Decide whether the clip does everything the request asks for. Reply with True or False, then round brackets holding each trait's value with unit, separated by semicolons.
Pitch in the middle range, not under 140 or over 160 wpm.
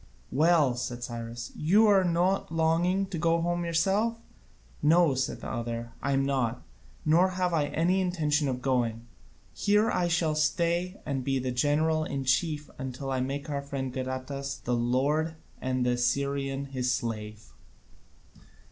True (145 Hz; 150 wpm)